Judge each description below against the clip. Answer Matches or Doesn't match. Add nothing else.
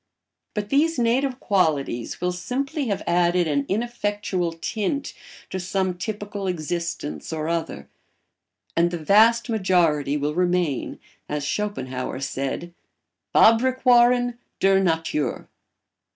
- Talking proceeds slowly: Matches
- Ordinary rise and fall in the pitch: Doesn't match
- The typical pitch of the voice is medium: Matches